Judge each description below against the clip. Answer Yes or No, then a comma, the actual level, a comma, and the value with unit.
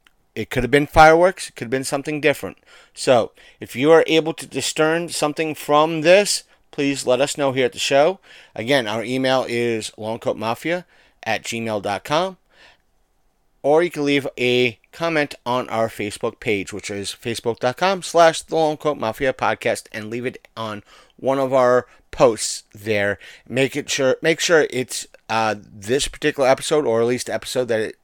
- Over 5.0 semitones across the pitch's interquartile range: Yes, wide, 5.4 semitones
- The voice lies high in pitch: No, low, 130 Hz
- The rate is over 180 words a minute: No, average, 170 wpm